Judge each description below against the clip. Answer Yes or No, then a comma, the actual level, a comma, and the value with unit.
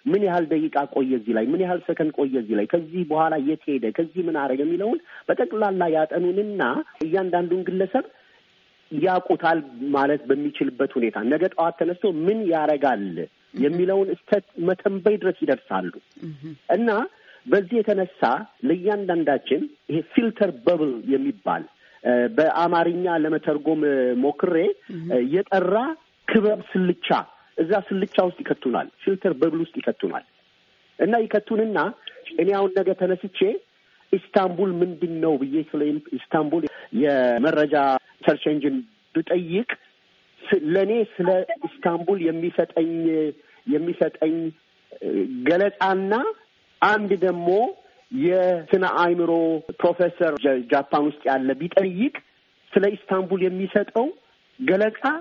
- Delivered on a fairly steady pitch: No, average, 4.7 semitones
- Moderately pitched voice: Yes, medium, 180 Hz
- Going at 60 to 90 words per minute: No, average, 100 wpm